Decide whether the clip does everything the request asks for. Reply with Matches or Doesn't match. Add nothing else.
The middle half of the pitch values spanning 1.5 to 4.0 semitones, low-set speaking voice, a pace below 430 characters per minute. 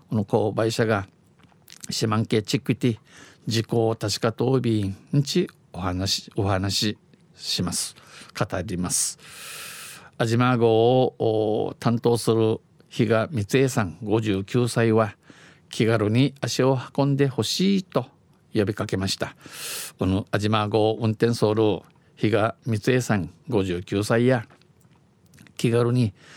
Matches